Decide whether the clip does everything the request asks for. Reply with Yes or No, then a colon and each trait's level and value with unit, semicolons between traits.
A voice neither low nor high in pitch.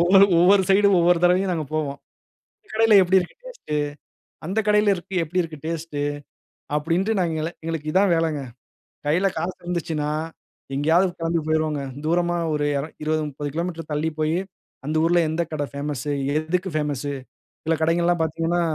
Yes: medium, 165 Hz